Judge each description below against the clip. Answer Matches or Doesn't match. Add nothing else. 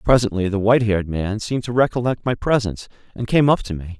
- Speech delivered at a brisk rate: Matches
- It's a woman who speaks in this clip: Doesn't match